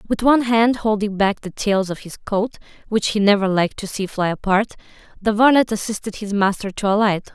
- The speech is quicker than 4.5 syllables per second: No, 4.4 syllables/s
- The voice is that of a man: No, female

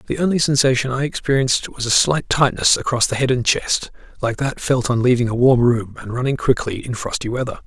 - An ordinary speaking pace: No, fast, 220 wpm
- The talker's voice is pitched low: Yes, low, 125 Hz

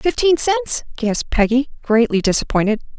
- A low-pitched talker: No, high, 240 Hz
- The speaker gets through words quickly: No, slow, 120 wpm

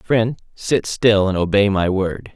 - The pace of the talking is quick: No, average, 180 wpm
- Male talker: Yes, male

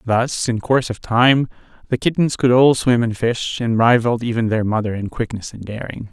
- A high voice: No, low, 115 Hz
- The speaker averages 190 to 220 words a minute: Yes, fast, 205 wpm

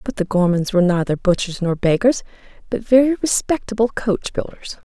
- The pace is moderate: Yes, average, 160 wpm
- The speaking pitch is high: Yes, high, 205 Hz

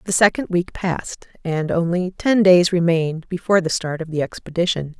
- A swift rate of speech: No, average, 180 wpm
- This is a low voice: No, medium, 175 Hz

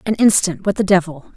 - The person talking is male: No, female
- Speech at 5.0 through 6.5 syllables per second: Yes, 5.7 syllables/s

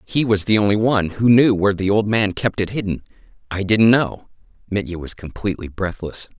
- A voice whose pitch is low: Yes, low, 100 Hz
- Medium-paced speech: Yes, average, 195 wpm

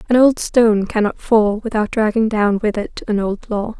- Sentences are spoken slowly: No, fast, 205 wpm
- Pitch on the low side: No, high, 215 Hz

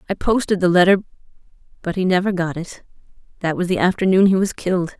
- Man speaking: No, female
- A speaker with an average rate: Yes, average, 190 wpm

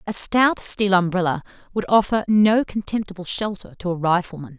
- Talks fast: No, average, 155 wpm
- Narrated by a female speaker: Yes, female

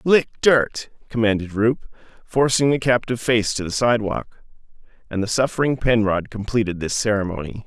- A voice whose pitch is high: No, low, 115 Hz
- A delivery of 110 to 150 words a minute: Yes, average, 140 wpm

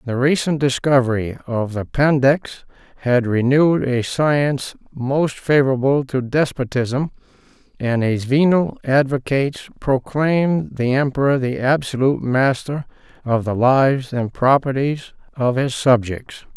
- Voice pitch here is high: No, low, 135 Hz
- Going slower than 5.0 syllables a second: Yes, 4.3 syllables/s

